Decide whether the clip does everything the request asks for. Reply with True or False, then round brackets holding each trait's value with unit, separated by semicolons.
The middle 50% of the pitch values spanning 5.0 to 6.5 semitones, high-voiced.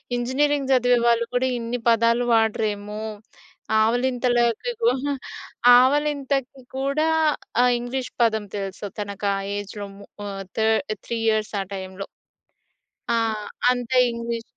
False (3.2 semitones; 235 Hz)